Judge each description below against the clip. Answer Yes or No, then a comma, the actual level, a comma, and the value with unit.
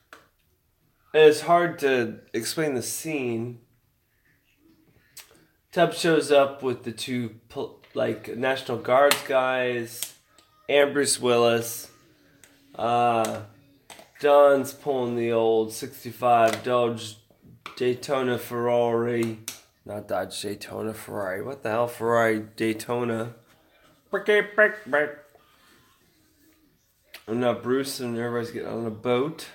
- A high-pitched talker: No, low, 120 Hz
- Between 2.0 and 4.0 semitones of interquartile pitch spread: Yes, average, 3.3 semitones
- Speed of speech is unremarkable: No, slow, 95 wpm